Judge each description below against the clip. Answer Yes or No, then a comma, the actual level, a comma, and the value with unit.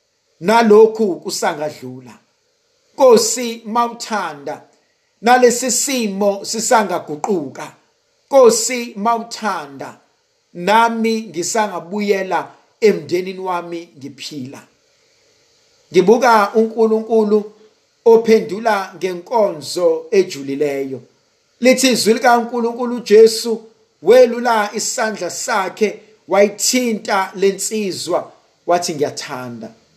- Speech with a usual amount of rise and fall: Yes, average, 4.1 semitones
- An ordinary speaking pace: No, slow, 65 wpm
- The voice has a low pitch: No, high, 220 Hz